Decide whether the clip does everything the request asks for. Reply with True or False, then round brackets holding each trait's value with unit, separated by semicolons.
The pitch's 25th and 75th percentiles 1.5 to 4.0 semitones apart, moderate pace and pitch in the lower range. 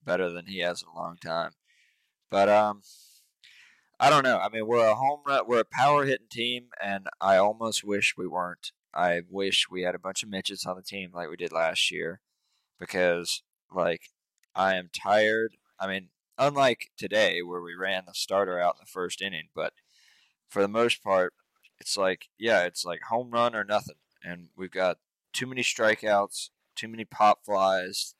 True (3.4 semitones; 190 wpm; 100 Hz)